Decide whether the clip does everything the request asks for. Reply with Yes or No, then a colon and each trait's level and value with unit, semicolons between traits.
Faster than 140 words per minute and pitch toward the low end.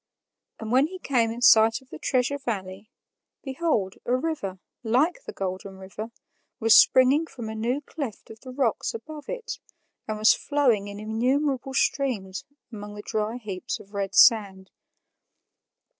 No: average, 155 wpm; high, 230 Hz